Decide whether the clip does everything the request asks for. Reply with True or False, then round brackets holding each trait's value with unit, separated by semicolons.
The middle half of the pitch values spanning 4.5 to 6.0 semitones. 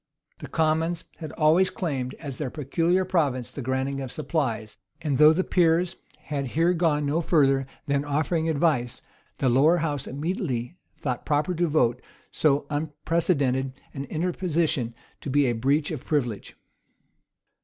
False (3.5 semitones)